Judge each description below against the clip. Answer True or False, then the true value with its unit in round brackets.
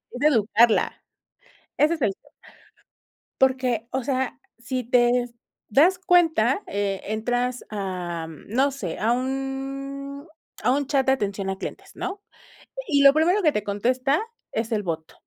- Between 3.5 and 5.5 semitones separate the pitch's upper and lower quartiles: True (4.5 semitones)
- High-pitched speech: True (255 Hz)